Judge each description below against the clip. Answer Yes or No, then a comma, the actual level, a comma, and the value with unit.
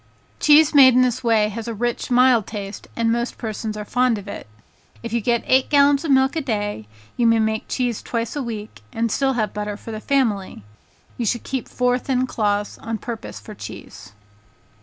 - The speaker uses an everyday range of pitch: Yes, average, 3.1 semitones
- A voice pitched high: Yes, high, 230 Hz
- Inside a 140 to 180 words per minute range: No, average, 200 wpm